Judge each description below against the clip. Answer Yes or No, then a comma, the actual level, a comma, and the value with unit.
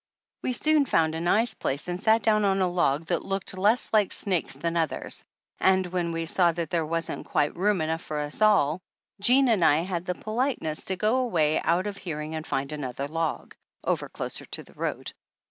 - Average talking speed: No, fast, 210 wpm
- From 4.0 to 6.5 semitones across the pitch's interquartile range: Yes, average, 4.4 semitones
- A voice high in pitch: No, medium, 175 Hz